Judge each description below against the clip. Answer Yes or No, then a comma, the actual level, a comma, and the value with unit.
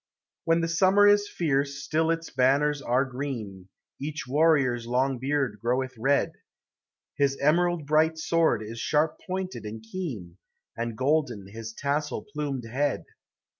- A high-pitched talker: No, medium, 140 Hz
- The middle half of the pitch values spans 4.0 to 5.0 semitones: Yes, average, 4.7 semitones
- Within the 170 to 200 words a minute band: No, slow, 135 wpm